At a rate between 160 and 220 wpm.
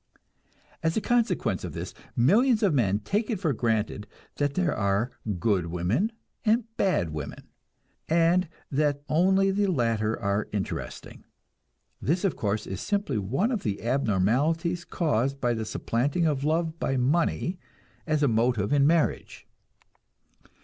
No: average, 145 wpm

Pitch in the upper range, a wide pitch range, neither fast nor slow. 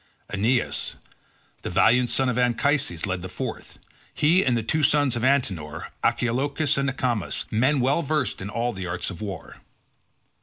No: low, 125 Hz; wide, 5.7 semitones; average, 160 wpm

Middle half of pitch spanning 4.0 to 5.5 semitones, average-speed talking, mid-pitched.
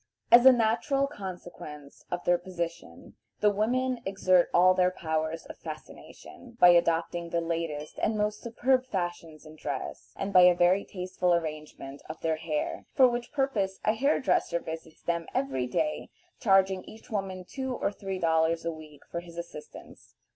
Yes: average, 4.4 semitones; average, 165 wpm; medium, 180 Hz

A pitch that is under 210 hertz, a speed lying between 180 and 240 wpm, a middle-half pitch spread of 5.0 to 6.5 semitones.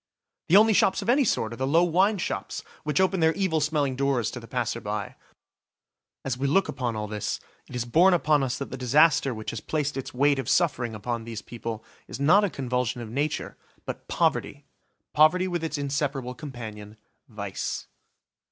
Yes: low, 135 Hz; average, 190 wpm; average, 5.3 semitones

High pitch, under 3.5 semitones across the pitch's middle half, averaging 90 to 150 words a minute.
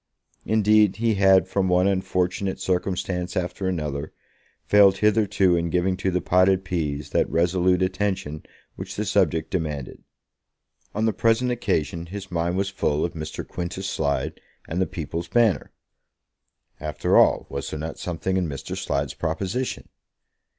No: very low, 90 Hz; average, 2.8 semitones; average, 145 wpm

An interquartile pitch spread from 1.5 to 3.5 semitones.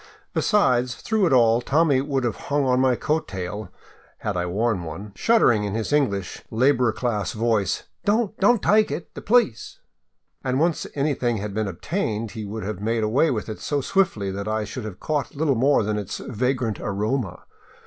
No: wide, 5.4 semitones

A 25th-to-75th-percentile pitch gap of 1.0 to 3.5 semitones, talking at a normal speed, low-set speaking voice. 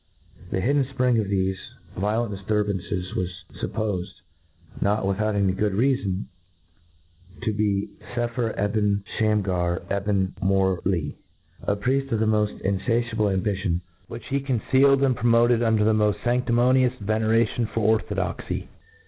No: average, 3.1 semitones; slow, 130 wpm; low, 105 Hz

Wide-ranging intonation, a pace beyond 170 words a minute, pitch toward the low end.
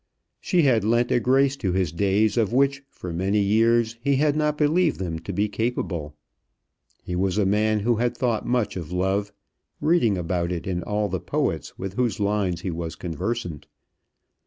No: average, 4.9 semitones; average, 185 wpm; low, 105 Hz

